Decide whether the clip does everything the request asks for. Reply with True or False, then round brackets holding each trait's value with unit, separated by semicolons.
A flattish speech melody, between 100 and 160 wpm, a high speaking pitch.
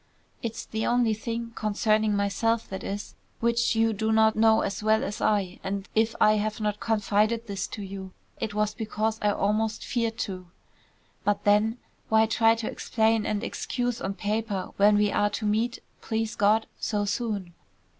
False (1.5 semitones; 175 wpm; 215 Hz)